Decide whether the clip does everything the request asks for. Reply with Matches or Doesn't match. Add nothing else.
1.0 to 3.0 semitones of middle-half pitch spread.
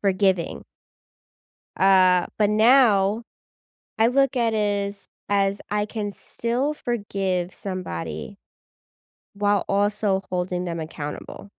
Matches